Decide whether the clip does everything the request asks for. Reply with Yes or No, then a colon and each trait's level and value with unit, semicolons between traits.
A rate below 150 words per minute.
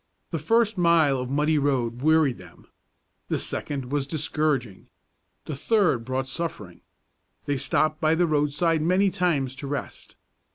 Yes: average, 140 wpm